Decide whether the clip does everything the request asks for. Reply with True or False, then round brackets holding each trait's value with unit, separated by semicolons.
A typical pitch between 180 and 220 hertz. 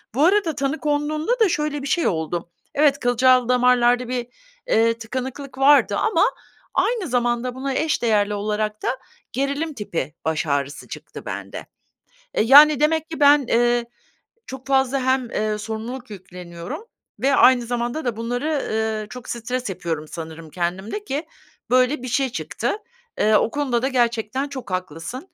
False (250 Hz)